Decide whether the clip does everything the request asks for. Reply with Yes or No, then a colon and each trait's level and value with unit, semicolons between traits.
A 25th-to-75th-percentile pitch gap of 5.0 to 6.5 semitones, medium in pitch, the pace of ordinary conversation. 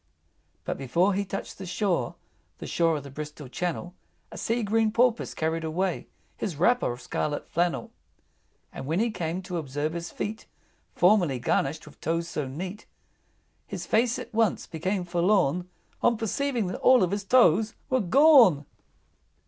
Yes: average, 5.3 semitones; medium, 180 Hz; average, 160 wpm